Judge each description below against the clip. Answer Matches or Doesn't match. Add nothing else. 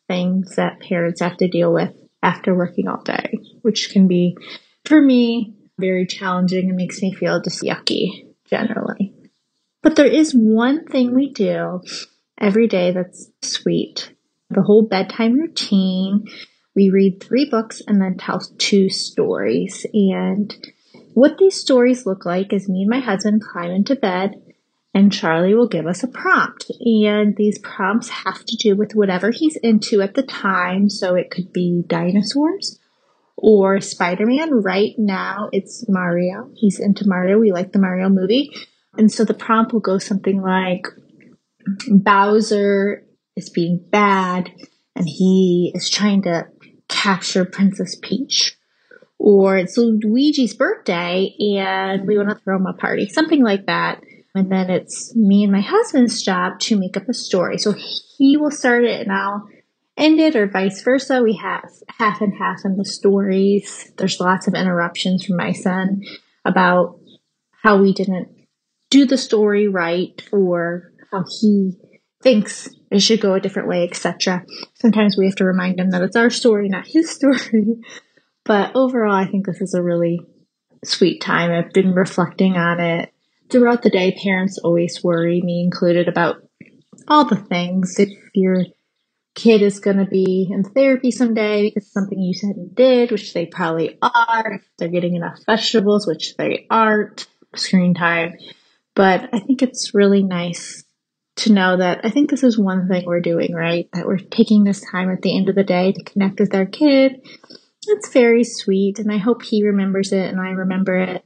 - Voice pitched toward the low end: Doesn't match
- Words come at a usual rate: Matches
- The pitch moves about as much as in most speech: Matches